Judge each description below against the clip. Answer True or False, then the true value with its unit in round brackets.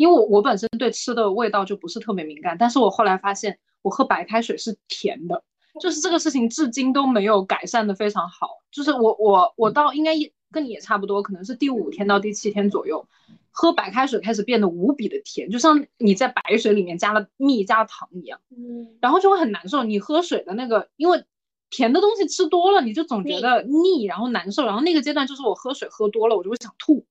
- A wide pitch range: True (6.3 semitones)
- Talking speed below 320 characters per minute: False (345 characters per minute)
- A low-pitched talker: False (235 Hz)